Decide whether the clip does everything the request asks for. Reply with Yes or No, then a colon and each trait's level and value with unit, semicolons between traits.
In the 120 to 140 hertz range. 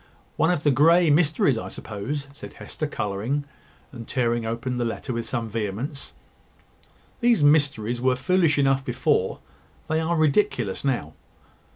Yes: low, 135 Hz